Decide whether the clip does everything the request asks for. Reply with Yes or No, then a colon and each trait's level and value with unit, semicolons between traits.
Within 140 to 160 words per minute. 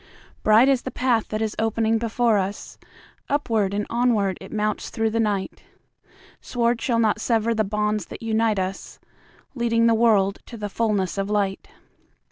Yes: average, 150 wpm